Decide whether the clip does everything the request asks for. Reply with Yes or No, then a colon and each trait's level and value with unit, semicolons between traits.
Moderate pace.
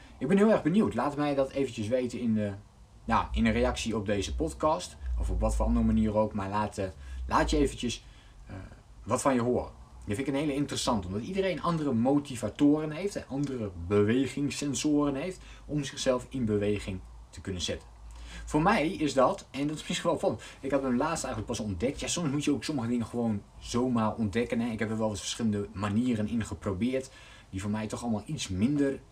No: fast, 205 wpm